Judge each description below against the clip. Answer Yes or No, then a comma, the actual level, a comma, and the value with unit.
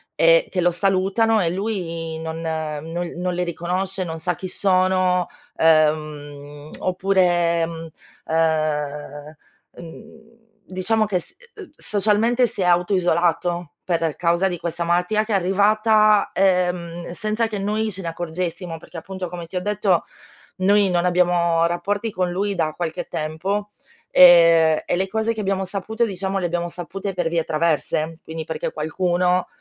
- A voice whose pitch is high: No, medium, 180 Hz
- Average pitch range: Yes, average, 3.0 semitones